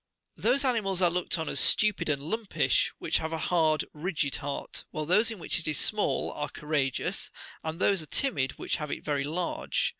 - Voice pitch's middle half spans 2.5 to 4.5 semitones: No, average, 4.9 semitones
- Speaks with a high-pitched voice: No, medium, 160 Hz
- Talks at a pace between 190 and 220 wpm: Yes, average, 200 wpm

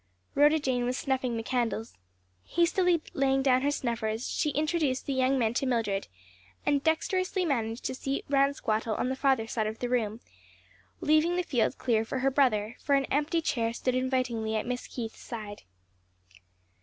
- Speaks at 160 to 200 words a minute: Yes, average, 170 wpm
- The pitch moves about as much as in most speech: Yes, average, 3.8 semitones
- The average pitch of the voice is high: Yes, very high, 260 Hz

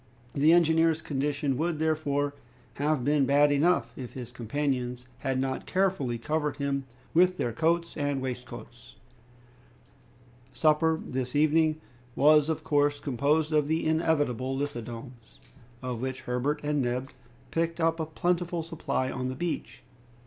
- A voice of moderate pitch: Yes, medium, 145 Hz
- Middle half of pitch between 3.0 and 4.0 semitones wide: Yes, average, 3.5 semitones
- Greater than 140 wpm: No, slow, 135 wpm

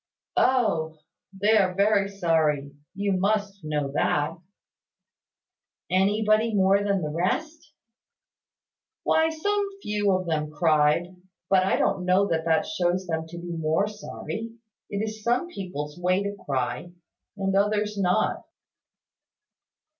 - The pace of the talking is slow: Yes, slow, 125 wpm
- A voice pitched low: No, high, 190 Hz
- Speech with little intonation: No, average, 4.4 semitones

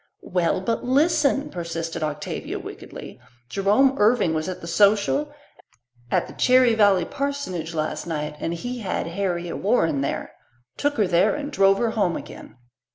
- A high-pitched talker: Yes, high, 195 Hz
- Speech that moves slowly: No, average, 155 wpm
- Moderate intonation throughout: No, wide, 6.8 semitones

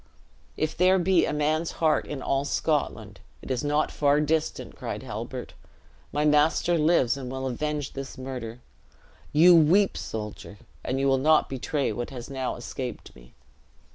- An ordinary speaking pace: Yes, average, 160 wpm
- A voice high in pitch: No, medium, 145 Hz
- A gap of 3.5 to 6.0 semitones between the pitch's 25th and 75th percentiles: No, average, 3.1 semitones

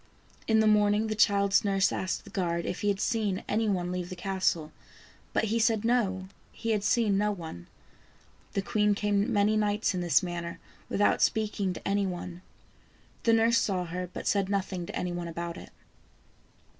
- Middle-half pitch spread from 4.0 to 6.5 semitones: No, average, 2.8 semitones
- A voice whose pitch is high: Yes, high, 200 Hz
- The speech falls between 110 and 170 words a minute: No, average, 185 wpm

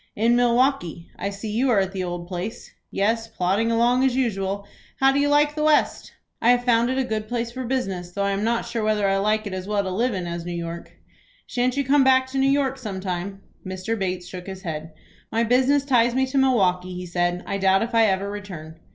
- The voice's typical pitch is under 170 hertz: No, high, 215 Hz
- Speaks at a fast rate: Yes, fast, 240 wpm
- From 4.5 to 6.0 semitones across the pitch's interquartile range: Yes, average, 4.9 semitones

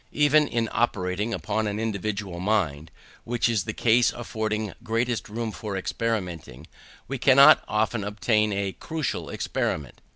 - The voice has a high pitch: No, low, 110 Hz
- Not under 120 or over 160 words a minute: Yes, slow, 135 wpm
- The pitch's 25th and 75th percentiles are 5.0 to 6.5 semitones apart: No, average, 3.1 semitones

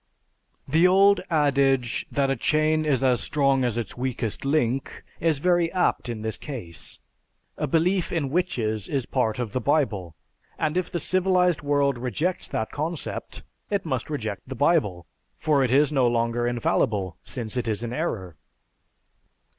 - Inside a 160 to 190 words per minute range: Yes, average, 165 wpm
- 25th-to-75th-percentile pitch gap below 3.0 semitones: No, average, 4.9 semitones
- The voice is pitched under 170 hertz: Yes, low, 135 Hz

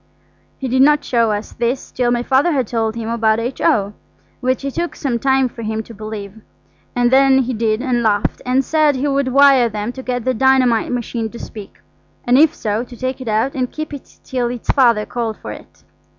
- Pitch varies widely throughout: No, average, 2.9 semitones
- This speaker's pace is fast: Yes, fast, 215 wpm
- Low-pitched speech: No, high, 245 Hz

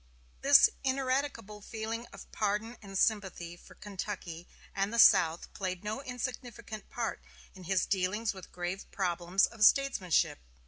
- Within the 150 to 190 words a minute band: No, slow, 135 wpm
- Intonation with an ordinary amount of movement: Yes, average, 3.9 semitones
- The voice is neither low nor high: No, high, 205 Hz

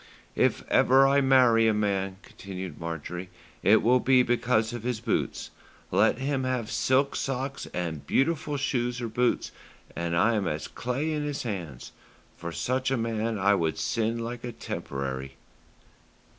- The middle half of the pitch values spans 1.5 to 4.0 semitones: No, wide, 5.4 semitones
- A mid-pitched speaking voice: No, low, 115 Hz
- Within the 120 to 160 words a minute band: Yes, average, 155 wpm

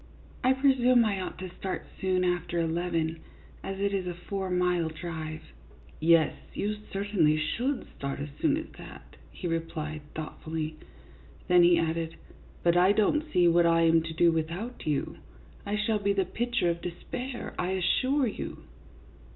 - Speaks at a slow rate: No, average, 165 wpm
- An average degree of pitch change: Yes, average, 3.8 semitones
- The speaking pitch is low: No, medium, 180 Hz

